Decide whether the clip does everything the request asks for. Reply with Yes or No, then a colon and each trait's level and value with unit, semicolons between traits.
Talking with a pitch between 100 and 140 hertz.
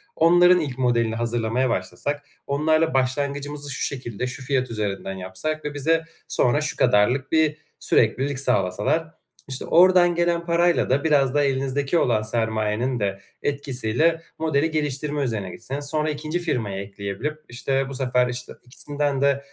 Yes: low, 135 Hz